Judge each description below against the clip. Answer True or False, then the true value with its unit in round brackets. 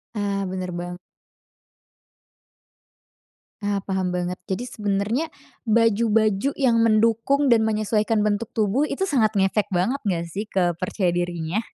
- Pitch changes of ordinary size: True (3.2 semitones)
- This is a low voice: False (210 Hz)